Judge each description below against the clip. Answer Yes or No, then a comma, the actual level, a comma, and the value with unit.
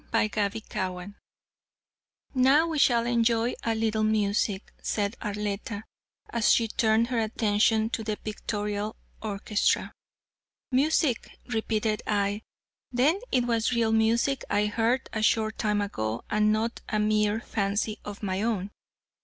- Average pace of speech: No, slow, 130 wpm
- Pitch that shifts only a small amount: Yes, narrow, 2.0 semitones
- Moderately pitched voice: No, high, 220 Hz